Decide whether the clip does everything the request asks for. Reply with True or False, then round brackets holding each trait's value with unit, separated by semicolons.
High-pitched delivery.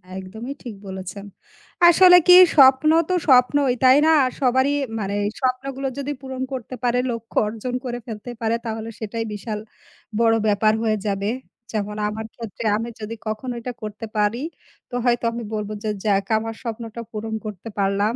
True (225 Hz)